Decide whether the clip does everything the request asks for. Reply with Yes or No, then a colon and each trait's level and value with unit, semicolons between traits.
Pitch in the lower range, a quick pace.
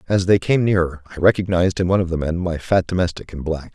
Yes: very low, 90 Hz; fast, 255 wpm